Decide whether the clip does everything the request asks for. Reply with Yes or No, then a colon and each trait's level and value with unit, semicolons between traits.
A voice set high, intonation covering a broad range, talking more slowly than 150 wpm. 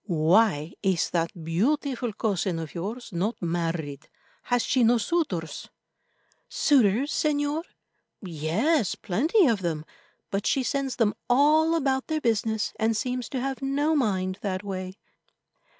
Yes: high, 225 Hz; wide, 6.8 semitones; slow, 135 wpm